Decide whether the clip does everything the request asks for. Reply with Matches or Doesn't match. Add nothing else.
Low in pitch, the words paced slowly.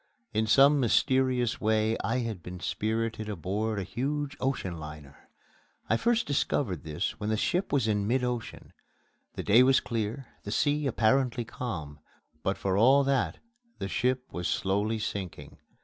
Doesn't match